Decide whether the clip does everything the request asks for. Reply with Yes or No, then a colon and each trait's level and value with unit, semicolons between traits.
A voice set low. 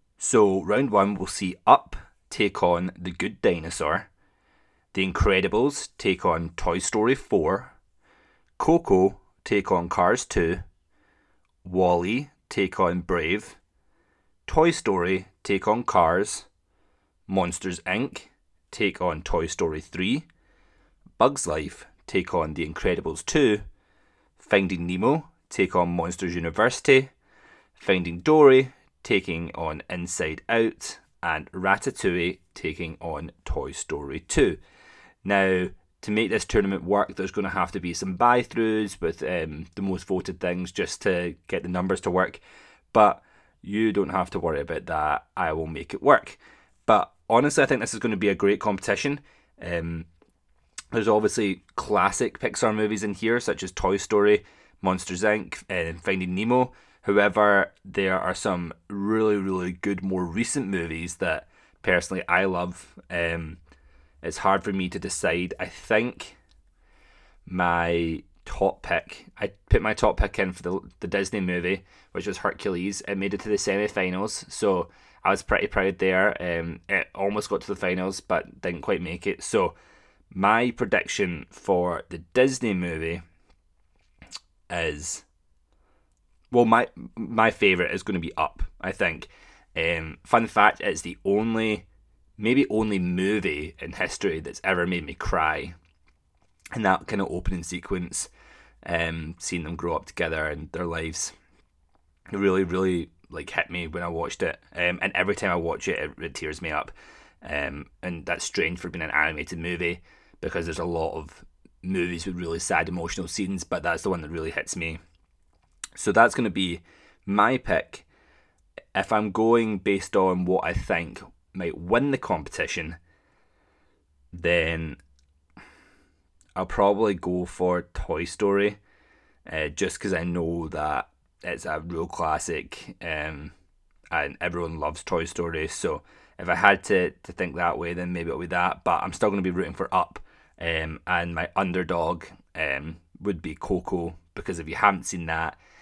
Yes: very low, 90 Hz